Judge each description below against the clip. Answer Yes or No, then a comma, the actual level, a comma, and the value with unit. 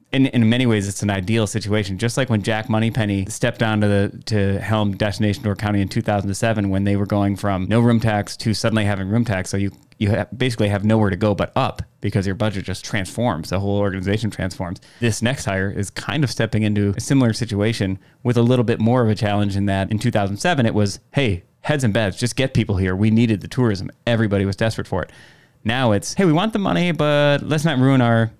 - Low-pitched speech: Yes, low, 110 Hz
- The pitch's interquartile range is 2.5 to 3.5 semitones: Yes, average, 2.8 semitones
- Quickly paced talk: Yes, fast, 245 wpm